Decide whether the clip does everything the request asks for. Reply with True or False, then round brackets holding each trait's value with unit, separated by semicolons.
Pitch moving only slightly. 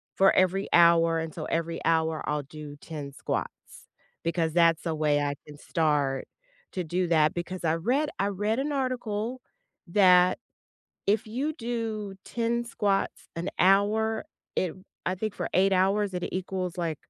False (4.4 semitones)